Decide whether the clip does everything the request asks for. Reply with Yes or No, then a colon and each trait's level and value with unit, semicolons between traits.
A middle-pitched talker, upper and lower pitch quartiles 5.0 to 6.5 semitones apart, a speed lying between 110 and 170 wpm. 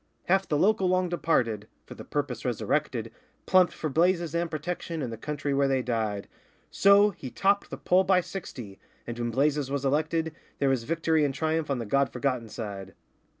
No: medium, 150 Hz; wide, 5.4 semitones; average, 190 wpm